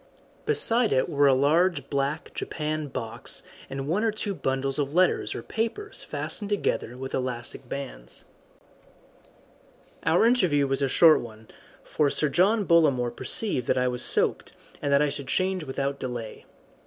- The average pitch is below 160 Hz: Yes, medium, 140 Hz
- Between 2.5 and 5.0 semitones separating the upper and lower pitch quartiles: No, wide, 5.5 semitones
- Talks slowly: No, average, 155 wpm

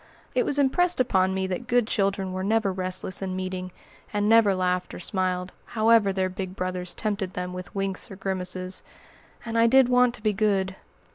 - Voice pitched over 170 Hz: Yes, high, 190 Hz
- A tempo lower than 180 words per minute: No, average, 190 wpm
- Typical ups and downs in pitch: Yes, average, 3.2 semitones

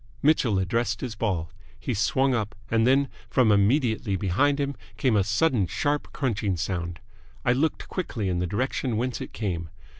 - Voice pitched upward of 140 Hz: No, low, 110 Hz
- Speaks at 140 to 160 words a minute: No, average, 170 wpm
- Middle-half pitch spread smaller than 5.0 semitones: No, average, 5.3 semitones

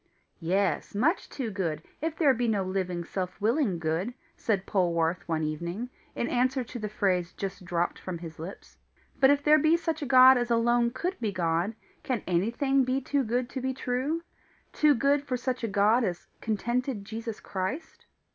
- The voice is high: Yes, high, 230 Hz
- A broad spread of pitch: Yes, wide, 6.0 semitones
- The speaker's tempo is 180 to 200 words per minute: Yes, average, 185 wpm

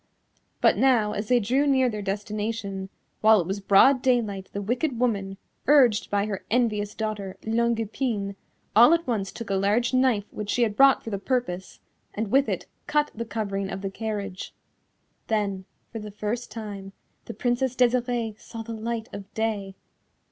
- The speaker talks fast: No, average, 175 wpm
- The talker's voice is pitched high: Yes, high, 220 Hz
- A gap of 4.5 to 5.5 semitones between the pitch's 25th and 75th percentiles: No, average, 3.3 semitones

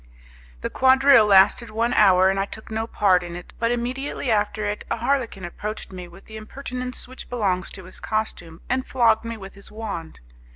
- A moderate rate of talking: Yes, average, 195 wpm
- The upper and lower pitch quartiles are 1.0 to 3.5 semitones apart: No, average, 3.9 semitones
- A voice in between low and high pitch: No, high, 215 Hz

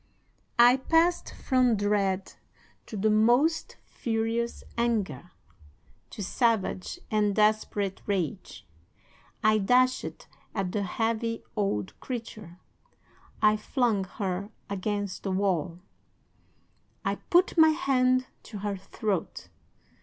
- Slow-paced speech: Yes, slow, 100 wpm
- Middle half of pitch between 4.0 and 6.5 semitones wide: No, average, 3.5 semitones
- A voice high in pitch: Yes, high, 215 Hz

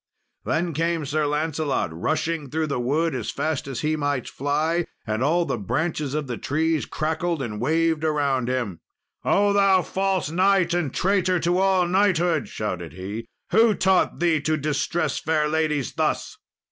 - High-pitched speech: No, medium, 155 Hz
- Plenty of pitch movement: No, average, 3.8 semitones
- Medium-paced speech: Yes, average, 160 wpm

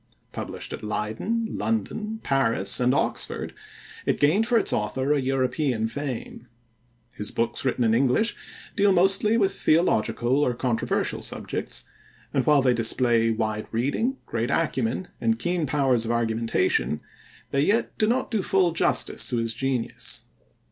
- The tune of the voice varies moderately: No, wide, 8.0 semitones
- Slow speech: No, average, 145 wpm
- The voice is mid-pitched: No, low, 130 Hz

